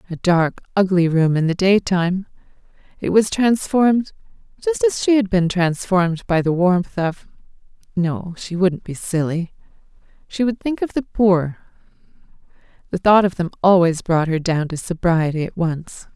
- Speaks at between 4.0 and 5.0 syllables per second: Yes, 4.6 syllables/s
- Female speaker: Yes, female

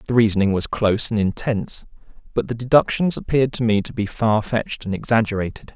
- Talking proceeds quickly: No, average, 190 wpm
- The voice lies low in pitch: Yes, low, 110 Hz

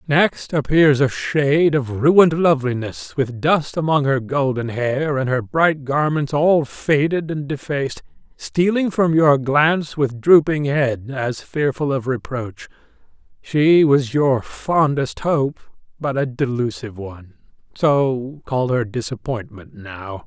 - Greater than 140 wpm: No, slow, 135 wpm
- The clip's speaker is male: Yes, male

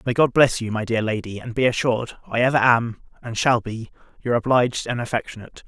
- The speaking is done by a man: Yes, male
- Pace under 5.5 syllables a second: No, 6.1 syllables/s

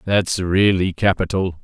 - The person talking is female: No, male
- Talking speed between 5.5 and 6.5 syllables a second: No, 4.0 syllables/s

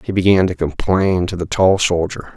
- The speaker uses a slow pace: No, fast, 205 wpm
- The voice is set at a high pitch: No, very low, 90 Hz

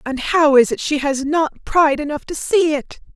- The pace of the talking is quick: Yes, fast, 230 wpm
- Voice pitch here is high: Yes, very high, 295 Hz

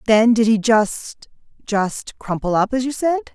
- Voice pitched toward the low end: No, high, 230 Hz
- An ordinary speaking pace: Yes, average, 145 wpm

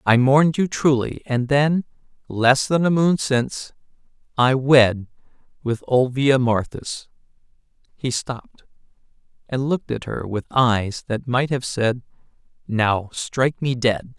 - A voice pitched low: Yes, low, 130 Hz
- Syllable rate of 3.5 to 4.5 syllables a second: Yes, 4.0 syllables/s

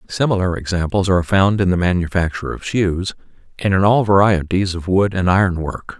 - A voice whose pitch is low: Yes, very low, 95 Hz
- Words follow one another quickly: No, average, 180 wpm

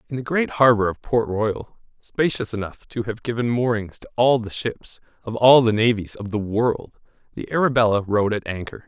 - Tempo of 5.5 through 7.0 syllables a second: No, 5.0 syllables/s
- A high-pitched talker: No, low, 115 Hz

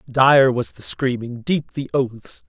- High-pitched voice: No, low, 130 Hz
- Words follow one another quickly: No, average, 145 wpm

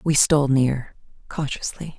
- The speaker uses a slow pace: Yes, slow, 120 wpm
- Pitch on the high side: No, medium, 140 Hz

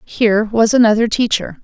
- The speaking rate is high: No, average, 145 wpm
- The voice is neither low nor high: No, high, 220 Hz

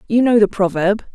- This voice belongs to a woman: Yes, female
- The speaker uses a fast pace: Yes, fast, 210 wpm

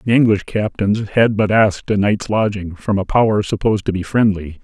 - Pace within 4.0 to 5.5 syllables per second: Yes, 5.4 syllables/s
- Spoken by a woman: No, male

